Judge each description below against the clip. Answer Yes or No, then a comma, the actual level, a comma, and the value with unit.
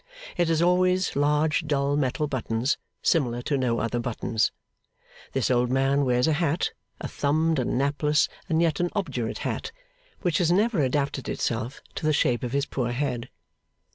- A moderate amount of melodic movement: Yes, average, 4.3 semitones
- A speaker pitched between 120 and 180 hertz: Yes, medium, 140 Hz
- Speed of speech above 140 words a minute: Yes, average, 170 wpm